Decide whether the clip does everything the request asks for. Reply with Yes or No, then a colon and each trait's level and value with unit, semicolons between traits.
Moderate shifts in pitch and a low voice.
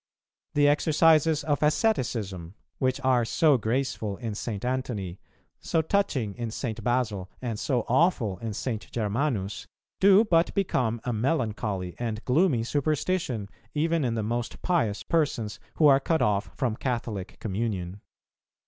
No: wide, 5.7 semitones; low, 120 Hz